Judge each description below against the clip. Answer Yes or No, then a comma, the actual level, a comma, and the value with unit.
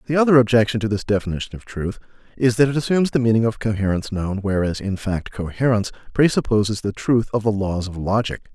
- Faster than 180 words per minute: Yes, fast, 205 wpm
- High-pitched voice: No, low, 110 Hz